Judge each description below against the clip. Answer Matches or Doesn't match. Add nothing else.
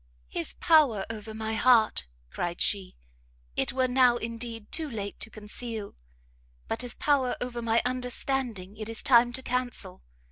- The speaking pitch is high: Matches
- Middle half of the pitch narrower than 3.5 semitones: Matches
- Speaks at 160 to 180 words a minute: Doesn't match